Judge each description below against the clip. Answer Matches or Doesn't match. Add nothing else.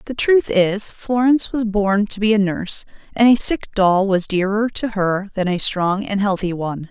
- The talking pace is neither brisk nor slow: Doesn't match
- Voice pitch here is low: Doesn't match